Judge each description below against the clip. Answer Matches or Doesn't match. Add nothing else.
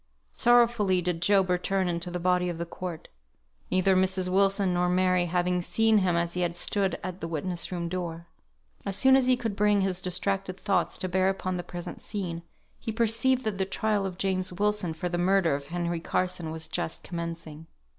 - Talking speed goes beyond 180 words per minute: Matches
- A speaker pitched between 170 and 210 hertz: Matches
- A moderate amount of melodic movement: Doesn't match